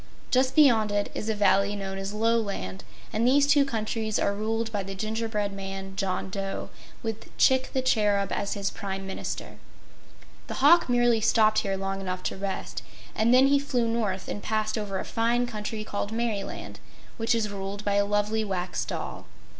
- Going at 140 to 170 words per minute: No, average, 180 wpm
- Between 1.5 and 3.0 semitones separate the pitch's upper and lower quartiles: Yes, narrow, 2.6 semitones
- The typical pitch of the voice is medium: No, high, 215 Hz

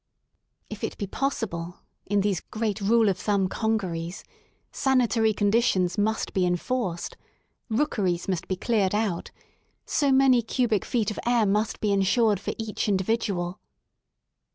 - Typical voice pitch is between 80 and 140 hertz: No, high, 210 Hz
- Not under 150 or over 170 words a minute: No, slow, 135 wpm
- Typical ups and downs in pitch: Yes, average, 3.5 semitones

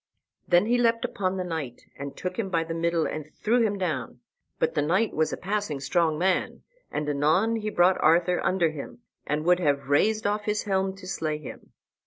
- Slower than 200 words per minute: No, fast, 205 wpm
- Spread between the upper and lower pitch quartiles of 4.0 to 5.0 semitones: Yes, average, 4.7 semitones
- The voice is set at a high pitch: No, medium, 180 Hz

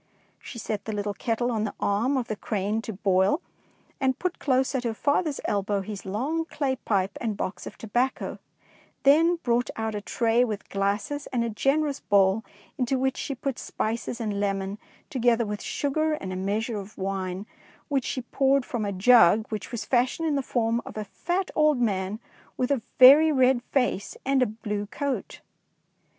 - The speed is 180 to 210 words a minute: Yes, average, 185 wpm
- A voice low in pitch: No, high, 235 Hz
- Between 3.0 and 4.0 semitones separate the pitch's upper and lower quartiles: No, average, 4.5 semitones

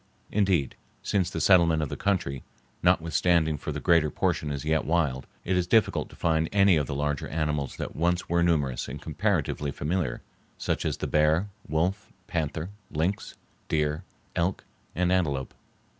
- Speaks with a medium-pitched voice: No, very low, 80 Hz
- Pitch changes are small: No, average, 3.2 semitones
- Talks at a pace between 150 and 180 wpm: Yes, average, 160 wpm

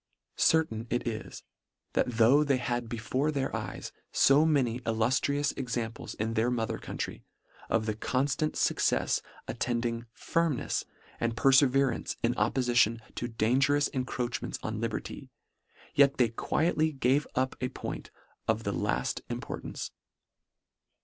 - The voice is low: Yes, low, 125 Hz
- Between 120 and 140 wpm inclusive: Yes, slow, 135 wpm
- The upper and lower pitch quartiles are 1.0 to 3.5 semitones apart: Yes, average, 3.2 semitones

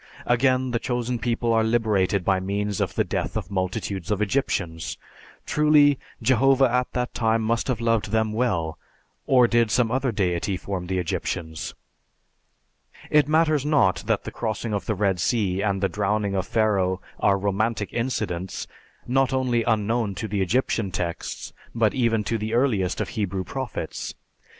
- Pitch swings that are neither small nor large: Yes, average, 3.9 semitones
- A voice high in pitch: No, low, 110 Hz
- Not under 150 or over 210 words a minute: Yes, average, 160 wpm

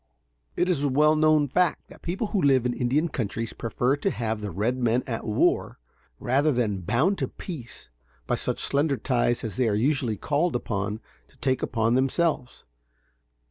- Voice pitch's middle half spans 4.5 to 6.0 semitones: Yes, average, 4.9 semitones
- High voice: No, low, 130 Hz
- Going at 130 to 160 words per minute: No, average, 180 wpm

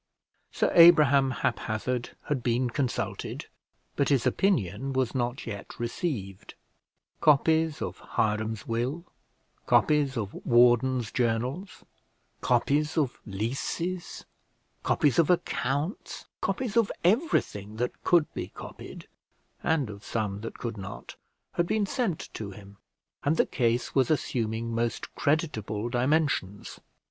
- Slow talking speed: Yes, slow, 115 wpm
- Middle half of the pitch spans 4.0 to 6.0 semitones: Yes, wide, 5.5 semitones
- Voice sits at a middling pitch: No, low, 125 Hz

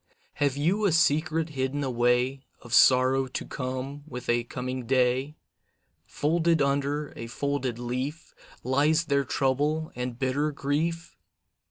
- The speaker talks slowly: Yes, slow, 130 wpm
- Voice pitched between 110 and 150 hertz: Yes, medium, 140 Hz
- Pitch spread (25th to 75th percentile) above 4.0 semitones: No, average, 2.8 semitones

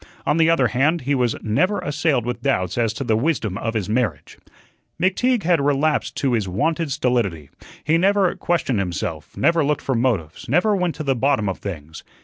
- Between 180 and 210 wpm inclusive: Yes, average, 190 wpm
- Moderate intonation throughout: No, wide, 6.9 semitones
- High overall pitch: No, low, 135 Hz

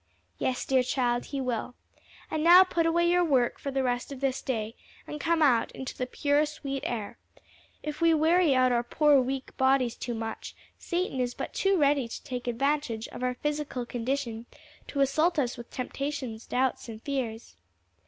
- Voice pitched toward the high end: Yes, very high, 265 Hz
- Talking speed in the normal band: Yes, average, 180 wpm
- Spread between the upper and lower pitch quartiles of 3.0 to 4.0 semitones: Yes, average, 3.4 semitones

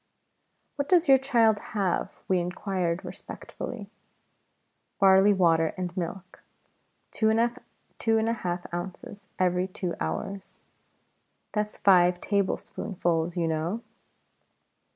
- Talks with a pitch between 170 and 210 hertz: Yes, high, 190 Hz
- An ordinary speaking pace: No, slow, 100 wpm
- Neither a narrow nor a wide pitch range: Yes, average, 3.5 semitones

